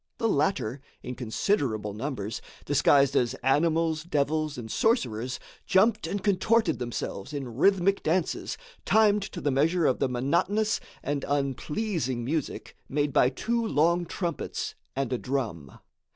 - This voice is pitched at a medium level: Yes, medium, 145 Hz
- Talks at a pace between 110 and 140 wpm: Yes, slow, 135 wpm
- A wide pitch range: Yes, wide, 6.6 semitones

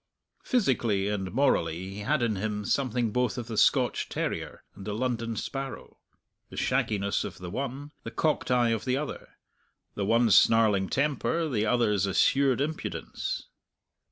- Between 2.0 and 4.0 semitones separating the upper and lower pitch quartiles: No, average, 4.4 semitones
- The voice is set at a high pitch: No, low, 115 Hz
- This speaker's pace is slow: No, average, 155 wpm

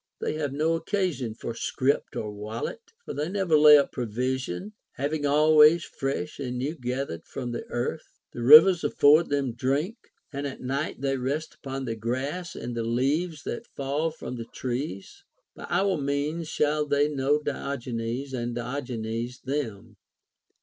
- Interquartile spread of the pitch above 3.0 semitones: Yes, average, 3.8 semitones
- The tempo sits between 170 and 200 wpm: No, average, 160 wpm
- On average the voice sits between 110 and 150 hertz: Yes, medium, 140 Hz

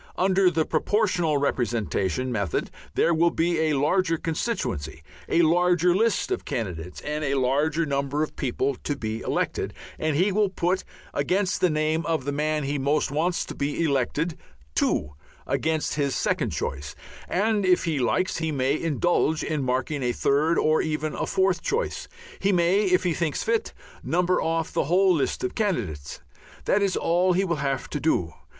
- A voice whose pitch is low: No, medium, 155 Hz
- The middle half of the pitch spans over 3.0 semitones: Yes, average, 4.4 semitones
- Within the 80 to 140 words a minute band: No, average, 175 wpm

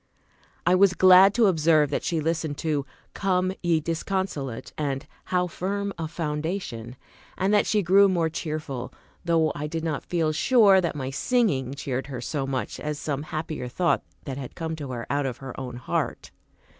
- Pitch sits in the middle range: Yes, medium, 160 Hz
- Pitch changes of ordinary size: Yes, average, 4.7 semitones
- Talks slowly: No, average, 180 wpm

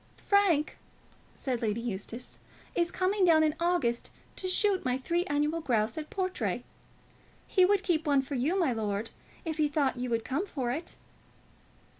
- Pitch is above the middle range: Yes, very high, 300 Hz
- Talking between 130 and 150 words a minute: No, average, 165 wpm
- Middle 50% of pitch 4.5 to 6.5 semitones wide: Yes, wide, 6.2 semitones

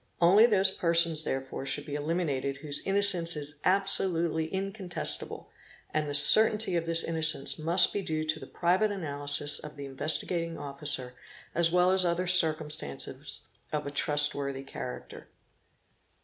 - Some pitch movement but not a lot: Yes, average, 3.8 semitones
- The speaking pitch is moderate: Yes, medium, 160 Hz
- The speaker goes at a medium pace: Yes, average, 150 wpm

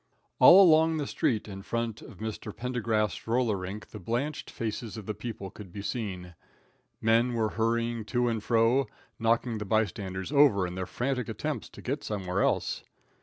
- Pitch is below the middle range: Yes, low, 110 Hz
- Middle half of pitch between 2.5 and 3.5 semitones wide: Yes, average, 2.9 semitones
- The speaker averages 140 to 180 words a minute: Yes, average, 170 wpm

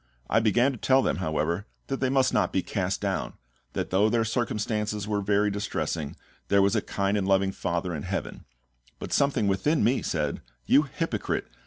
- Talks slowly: No, average, 185 wpm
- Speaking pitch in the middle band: No, low, 105 Hz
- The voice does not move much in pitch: No, average, 3.9 semitones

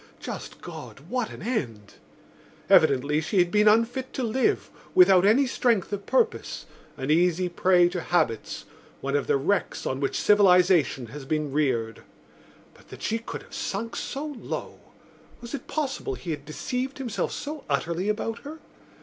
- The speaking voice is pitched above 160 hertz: Yes, medium, 185 Hz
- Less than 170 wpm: Yes, average, 160 wpm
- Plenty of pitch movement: Yes, wide, 8.0 semitones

